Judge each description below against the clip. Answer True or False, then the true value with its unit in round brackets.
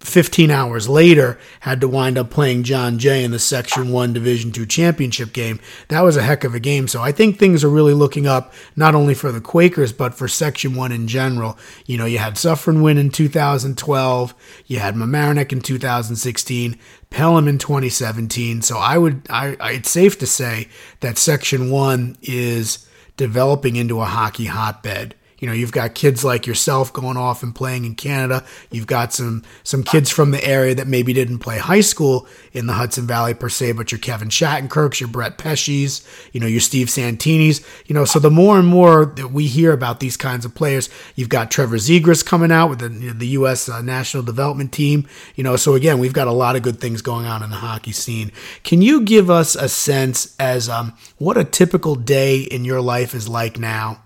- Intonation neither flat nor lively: True (3.4 semitones)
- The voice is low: True (130 Hz)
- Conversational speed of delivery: False (210 wpm)